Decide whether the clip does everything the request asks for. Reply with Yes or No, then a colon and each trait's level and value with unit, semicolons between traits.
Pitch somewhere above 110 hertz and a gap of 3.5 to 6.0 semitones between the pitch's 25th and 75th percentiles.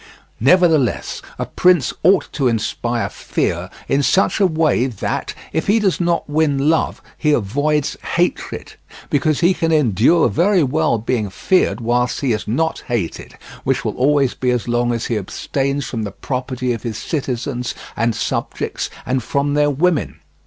Yes: low, 135 Hz; average, 4.8 semitones